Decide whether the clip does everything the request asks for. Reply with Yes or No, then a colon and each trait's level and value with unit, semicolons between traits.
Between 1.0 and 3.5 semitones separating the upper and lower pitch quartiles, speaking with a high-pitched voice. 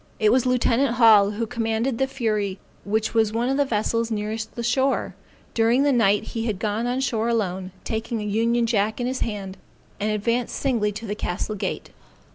Yes: narrow, 2.4 semitones; high, 225 Hz